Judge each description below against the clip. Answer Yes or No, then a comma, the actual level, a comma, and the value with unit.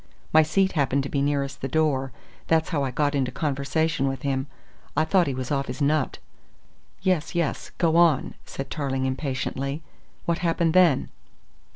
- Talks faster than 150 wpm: Yes, average, 170 wpm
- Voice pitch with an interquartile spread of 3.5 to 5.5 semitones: No, average, 3.0 semitones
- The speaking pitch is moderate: Yes, medium, 145 Hz